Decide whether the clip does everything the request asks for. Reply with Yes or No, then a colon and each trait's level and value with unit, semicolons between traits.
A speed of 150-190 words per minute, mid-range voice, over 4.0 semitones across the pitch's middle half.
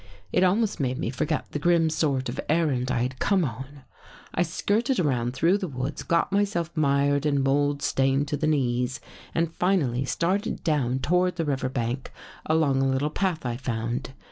Yes: average, 180 wpm; medium, 145 Hz; average, 4.4 semitones